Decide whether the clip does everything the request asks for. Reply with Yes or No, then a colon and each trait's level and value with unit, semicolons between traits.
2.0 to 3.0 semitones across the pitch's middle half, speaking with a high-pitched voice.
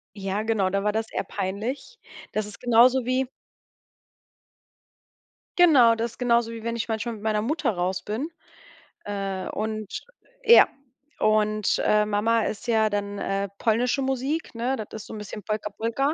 Yes: narrow, 2.6 semitones; high, 220 Hz